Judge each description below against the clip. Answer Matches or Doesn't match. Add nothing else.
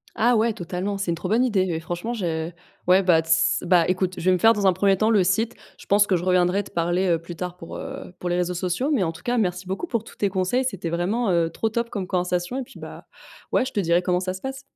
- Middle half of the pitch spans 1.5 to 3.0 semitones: Doesn't match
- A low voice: Doesn't match